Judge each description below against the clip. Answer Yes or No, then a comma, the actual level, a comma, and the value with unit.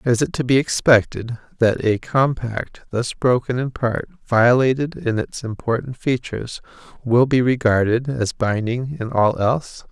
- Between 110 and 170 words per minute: Yes, average, 150 wpm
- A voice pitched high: No, low, 125 Hz